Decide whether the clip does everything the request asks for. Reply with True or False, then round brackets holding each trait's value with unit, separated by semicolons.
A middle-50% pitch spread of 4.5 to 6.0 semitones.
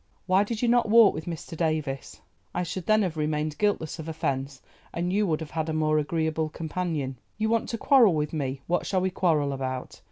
False (3.8 semitones)